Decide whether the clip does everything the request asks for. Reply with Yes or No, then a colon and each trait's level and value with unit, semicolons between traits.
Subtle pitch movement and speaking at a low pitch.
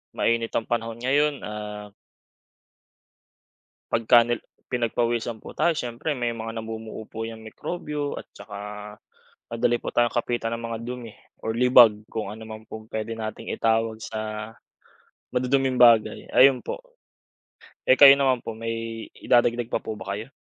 Yes: narrow, 1.8 semitones; low, 115 Hz